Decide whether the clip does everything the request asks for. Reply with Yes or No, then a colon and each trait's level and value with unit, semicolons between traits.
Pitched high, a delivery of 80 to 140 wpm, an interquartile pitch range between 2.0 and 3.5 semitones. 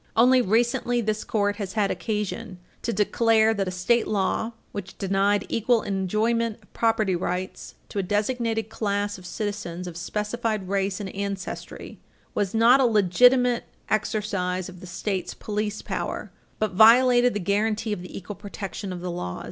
No: high, 210 Hz; average, 155 wpm; average, 2.7 semitones